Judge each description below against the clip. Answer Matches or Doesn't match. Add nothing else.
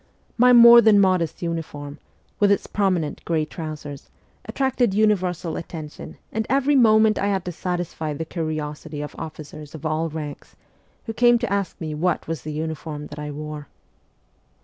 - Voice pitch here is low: Doesn't match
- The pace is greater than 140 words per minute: Matches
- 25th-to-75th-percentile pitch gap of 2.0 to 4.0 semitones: Doesn't match